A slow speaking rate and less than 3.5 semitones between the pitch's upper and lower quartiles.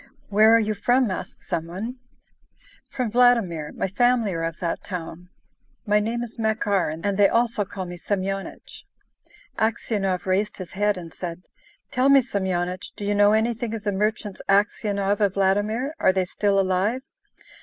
No: average, 165 wpm; average, 3.0 semitones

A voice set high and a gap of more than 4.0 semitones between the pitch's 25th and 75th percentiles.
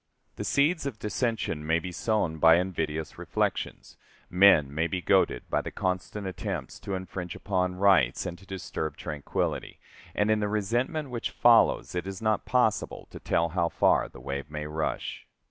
No: very low, 90 Hz; average, 4.7 semitones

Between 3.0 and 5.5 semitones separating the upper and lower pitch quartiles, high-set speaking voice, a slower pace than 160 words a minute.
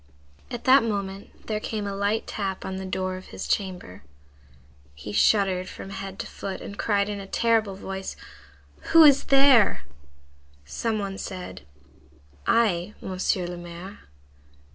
No: narrow, 2.4 semitones; high, 195 Hz; average, 145 wpm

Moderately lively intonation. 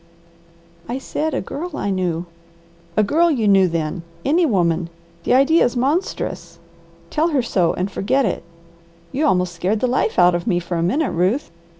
No: wide, 7.8 semitones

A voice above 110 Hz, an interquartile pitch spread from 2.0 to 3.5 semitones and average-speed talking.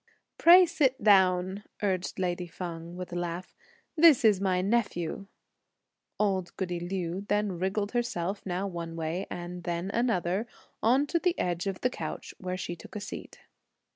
Yes: medium, 185 Hz; average, 3.0 semitones; average, 160 wpm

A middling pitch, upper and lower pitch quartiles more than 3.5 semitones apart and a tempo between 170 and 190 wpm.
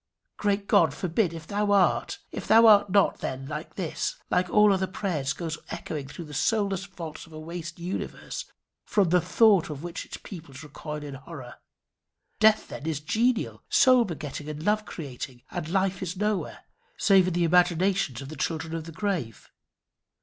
Yes: medium, 175 Hz; average, 4.5 semitones; average, 175 wpm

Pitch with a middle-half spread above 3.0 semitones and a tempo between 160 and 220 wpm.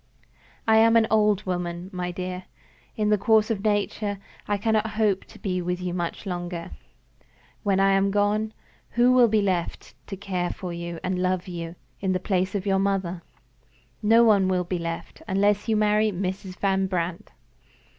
No: narrow, 2.6 semitones; average, 175 wpm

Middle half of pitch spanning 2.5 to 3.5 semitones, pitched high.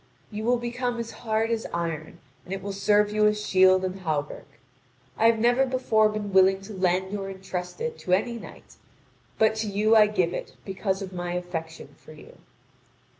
Yes: average, 3.0 semitones; high, 200 Hz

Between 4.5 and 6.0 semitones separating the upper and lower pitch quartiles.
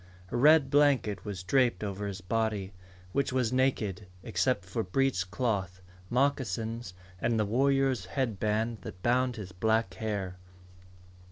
Yes: average, 4.9 semitones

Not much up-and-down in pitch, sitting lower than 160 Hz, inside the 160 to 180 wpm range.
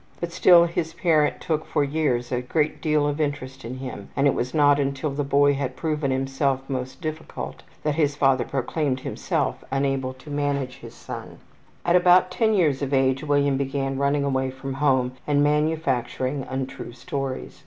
Yes: narrow, 2.3 semitones; medium, 140 Hz; average, 175 wpm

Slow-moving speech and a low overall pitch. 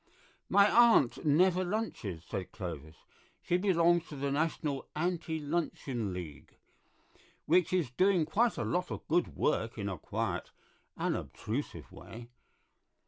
No: slow, 130 wpm; medium, 155 Hz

